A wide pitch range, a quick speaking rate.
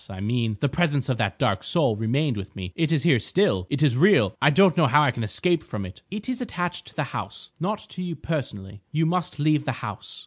Yes: wide, 7.4 semitones; fast, 245 wpm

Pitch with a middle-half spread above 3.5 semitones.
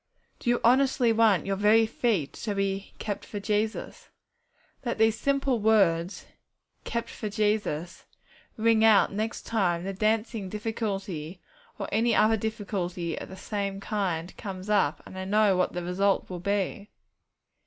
No: average, 2.7 semitones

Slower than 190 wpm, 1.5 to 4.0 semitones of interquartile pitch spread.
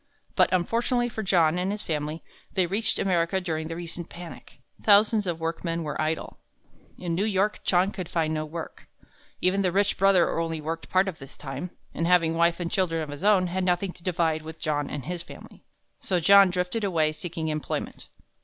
No: average, 195 wpm; average, 2.9 semitones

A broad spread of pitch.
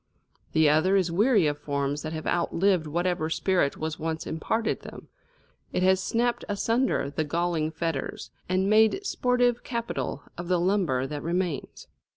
No: average, 4.4 semitones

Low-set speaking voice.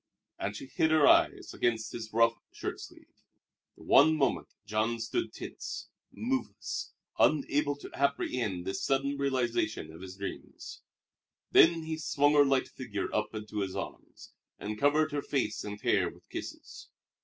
Yes: low, 130 Hz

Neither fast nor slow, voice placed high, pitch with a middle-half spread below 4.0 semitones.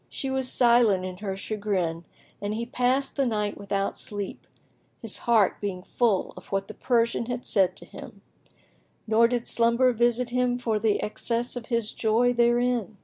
Yes: average, 170 wpm; high, 230 Hz; average, 3.1 semitones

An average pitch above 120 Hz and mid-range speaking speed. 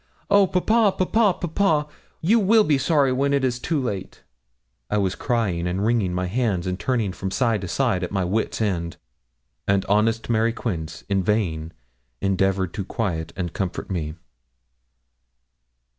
No: low, 105 Hz; average, 160 wpm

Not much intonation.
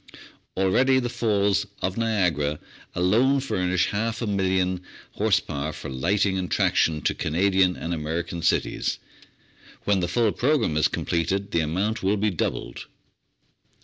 No: average, 3.8 semitones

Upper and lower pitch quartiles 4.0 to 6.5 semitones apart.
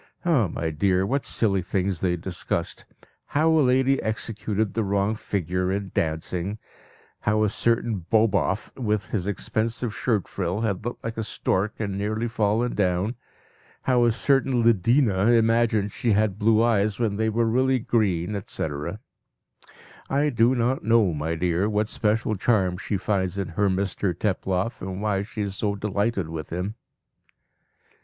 No: average, 3.2 semitones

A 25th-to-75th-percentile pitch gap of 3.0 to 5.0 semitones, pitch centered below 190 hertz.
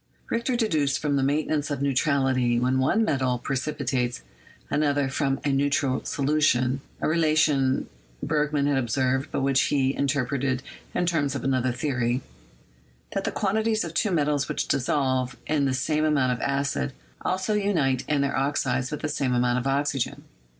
No: narrow, 2.5 semitones; medium, 140 Hz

